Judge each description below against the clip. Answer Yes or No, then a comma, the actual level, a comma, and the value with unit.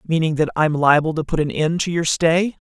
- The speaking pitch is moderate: Yes, medium, 160 Hz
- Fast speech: Yes, fast, 250 wpm